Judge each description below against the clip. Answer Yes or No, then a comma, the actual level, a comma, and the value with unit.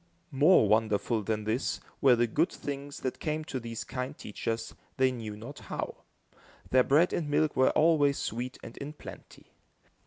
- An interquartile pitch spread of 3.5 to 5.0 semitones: Yes, average, 4.3 semitones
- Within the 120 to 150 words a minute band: No, average, 165 wpm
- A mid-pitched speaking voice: No, low, 130 Hz